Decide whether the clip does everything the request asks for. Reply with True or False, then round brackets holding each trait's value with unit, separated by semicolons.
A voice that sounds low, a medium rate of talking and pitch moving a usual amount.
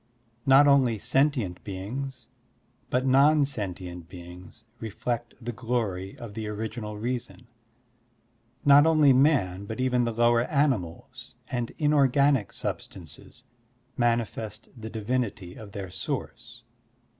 False (120 Hz; 115 wpm; 4.0 semitones)